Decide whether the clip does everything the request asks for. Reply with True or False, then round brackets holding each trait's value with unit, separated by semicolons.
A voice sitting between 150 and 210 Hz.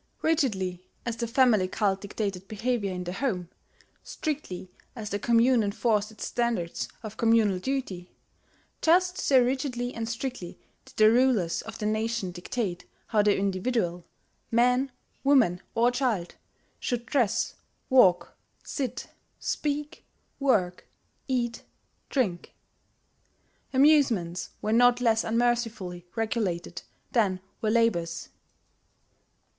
False (225 Hz)